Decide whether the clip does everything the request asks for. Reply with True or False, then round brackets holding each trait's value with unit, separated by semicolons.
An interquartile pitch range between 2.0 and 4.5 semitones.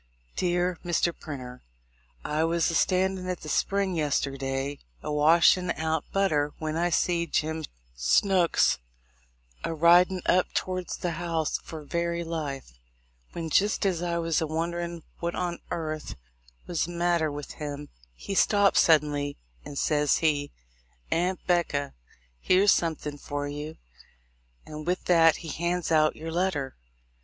True (2.8 semitones)